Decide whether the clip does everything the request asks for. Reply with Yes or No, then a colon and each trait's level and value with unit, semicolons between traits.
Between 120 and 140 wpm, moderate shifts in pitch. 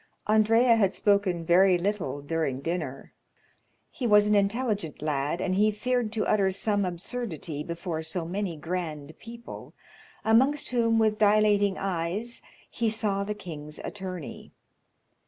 Yes: slow, 135 wpm; average, 4.4 semitones